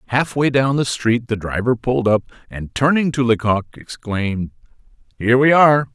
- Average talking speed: Yes, average, 160 wpm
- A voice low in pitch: Yes, low, 120 Hz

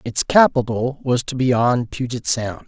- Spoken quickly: No, average, 180 wpm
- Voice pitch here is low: Yes, low, 125 Hz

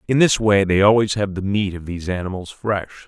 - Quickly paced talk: Yes, fast, 235 wpm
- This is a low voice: Yes, low, 100 Hz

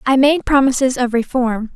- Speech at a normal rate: Yes, average, 170 wpm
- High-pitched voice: Yes, very high, 255 Hz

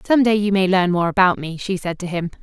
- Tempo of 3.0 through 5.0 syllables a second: No, 6.1 syllables/s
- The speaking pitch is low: No, high, 190 Hz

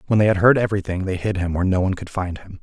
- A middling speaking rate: No, fast, 320 wpm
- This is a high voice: No, very low, 95 Hz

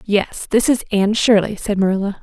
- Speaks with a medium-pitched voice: No, high, 205 Hz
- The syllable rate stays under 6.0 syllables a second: Yes, 5.5 syllables/s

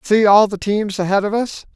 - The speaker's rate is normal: No, fast, 240 wpm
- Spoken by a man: Yes, male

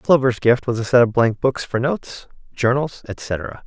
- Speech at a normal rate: Yes, average, 195 wpm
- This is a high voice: No, low, 125 Hz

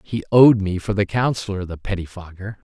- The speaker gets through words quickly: No, average, 175 wpm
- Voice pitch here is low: Yes, low, 100 Hz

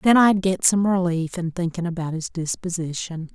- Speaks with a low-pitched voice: No, medium, 175 Hz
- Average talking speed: Yes, average, 180 wpm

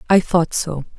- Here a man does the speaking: No, female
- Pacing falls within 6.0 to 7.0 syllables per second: No, 4.4 syllables/s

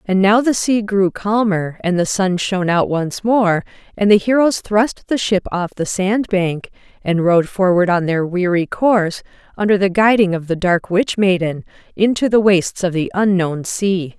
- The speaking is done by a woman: Yes, female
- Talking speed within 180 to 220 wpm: Yes, average, 190 wpm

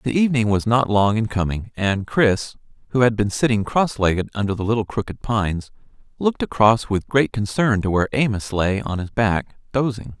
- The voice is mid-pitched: No, low, 110 Hz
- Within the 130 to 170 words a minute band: No, average, 195 wpm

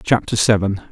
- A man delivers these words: Yes, male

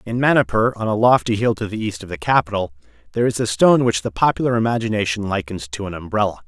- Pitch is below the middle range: Yes, low, 105 Hz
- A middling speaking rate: No, fast, 220 wpm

